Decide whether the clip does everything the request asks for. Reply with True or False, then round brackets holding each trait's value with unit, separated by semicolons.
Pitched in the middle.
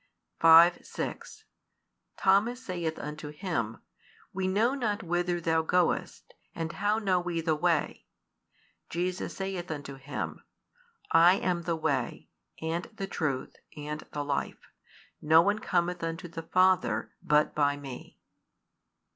True (170 Hz)